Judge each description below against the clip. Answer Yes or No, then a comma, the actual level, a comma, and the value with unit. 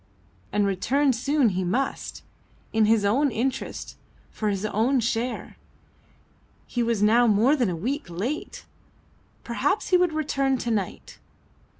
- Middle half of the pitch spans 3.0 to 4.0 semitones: No, average, 4.6 semitones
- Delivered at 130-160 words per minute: Yes, slow, 135 wpm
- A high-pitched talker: Yes, high, 235 Hz